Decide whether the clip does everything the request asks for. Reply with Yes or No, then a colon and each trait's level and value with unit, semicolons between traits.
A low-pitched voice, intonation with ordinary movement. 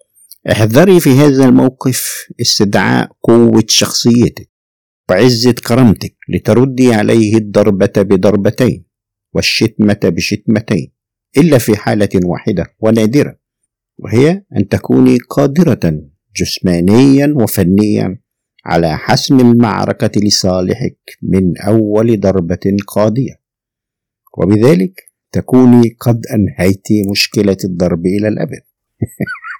Yes: low, 110 Hz; average, 4.2 semitones